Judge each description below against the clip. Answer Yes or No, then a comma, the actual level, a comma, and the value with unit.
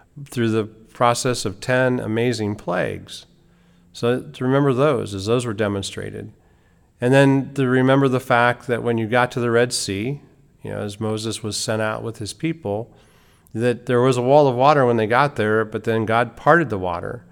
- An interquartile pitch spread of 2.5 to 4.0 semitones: Yes, average, 3.3 semitones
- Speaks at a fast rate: No, average, 195 wpm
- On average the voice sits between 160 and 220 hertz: No, low, 120 Hz